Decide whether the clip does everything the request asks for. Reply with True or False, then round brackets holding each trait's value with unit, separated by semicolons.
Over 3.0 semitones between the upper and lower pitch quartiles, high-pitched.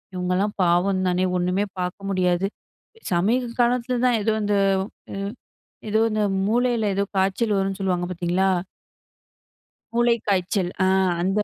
True (3.4 semitones; 195 Hz)